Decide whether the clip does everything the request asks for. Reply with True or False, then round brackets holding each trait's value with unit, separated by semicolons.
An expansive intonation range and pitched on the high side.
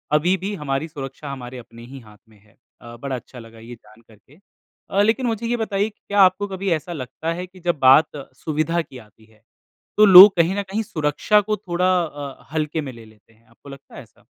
False (7.5 semitones; 150 Hz)